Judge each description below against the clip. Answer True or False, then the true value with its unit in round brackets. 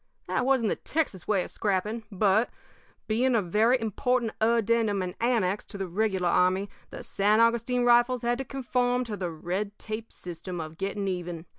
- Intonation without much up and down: False (4.1 semitones)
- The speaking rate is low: False (175 wpm)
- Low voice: False (215 Hz)